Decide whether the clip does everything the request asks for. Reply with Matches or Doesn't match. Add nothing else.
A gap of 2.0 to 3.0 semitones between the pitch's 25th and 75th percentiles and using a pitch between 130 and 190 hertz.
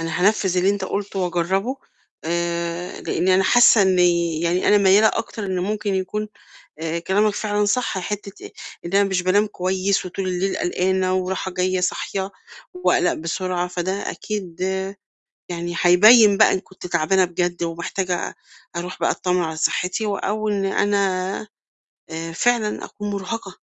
Matches